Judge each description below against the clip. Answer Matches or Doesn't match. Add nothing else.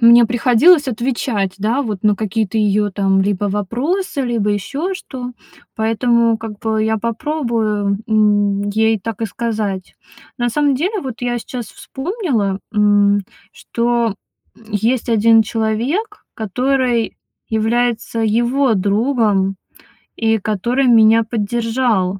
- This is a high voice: Matches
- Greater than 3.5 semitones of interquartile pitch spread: Doesn't match